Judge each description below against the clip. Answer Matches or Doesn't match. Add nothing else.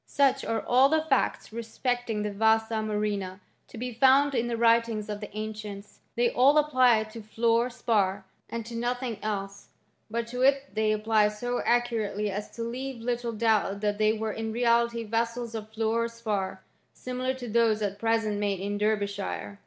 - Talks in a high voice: Matches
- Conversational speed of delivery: Matches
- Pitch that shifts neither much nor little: Doesn't match